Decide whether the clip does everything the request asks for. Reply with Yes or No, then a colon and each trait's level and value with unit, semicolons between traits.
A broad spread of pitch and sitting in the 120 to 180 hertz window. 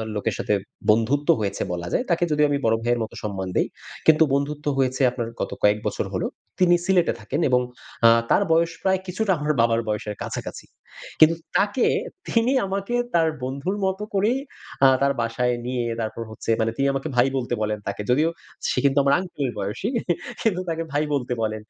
Yes: wide, 6.8 semitones; medium, 140 Hz